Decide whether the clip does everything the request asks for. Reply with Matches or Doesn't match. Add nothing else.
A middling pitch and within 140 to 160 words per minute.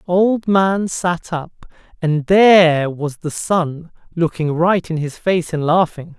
Matches